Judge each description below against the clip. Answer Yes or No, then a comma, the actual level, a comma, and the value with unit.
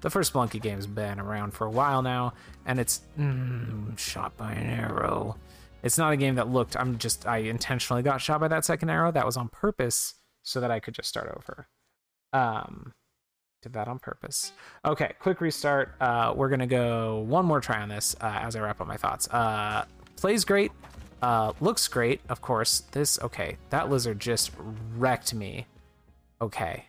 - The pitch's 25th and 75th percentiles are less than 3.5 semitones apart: No, average, 4.5 semitones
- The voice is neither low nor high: No, low, 120 Hz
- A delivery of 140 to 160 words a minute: No, average, 185 wpm